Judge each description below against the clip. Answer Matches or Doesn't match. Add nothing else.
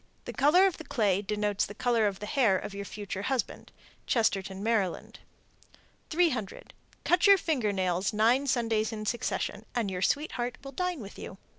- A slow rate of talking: Doesn't match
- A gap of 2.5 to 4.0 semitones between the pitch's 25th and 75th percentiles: Doesn't match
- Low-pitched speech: Doesn't match